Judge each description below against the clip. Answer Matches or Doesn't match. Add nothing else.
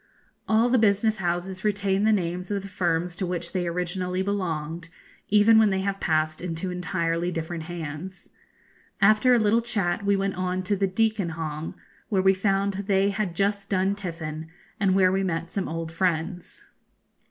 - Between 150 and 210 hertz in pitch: Matches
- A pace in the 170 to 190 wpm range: Matches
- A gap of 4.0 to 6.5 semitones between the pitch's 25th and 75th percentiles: Doesn't match